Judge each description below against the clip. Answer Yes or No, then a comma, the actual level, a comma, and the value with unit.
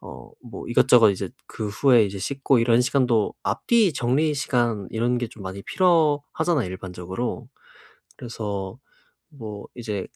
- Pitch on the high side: No, low, 120 Hz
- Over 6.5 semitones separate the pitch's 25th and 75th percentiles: No, average, 5.3 semitones